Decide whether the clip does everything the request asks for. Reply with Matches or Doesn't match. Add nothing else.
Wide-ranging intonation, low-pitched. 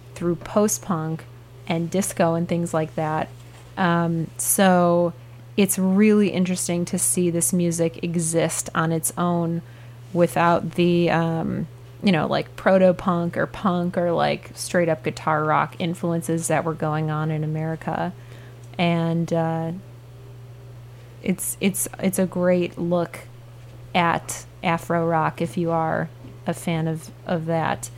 Doesn't match